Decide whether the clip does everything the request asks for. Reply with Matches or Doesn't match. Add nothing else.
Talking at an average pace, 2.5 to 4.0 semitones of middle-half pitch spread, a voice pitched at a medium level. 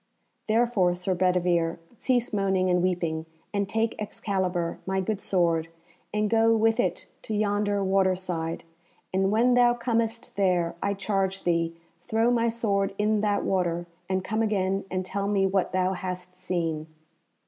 Doesn't match